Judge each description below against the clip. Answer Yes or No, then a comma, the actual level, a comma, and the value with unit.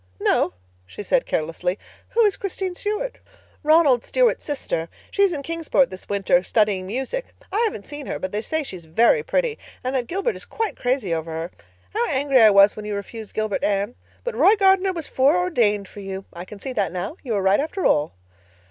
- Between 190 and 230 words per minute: Yes, average, 200 wpm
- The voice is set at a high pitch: Yes, very high, 250 Hz